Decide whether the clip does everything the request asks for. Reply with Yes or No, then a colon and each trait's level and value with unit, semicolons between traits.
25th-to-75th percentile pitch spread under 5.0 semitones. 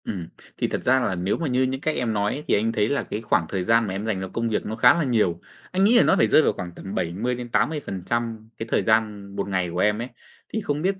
Yes: average, 4.6 semitones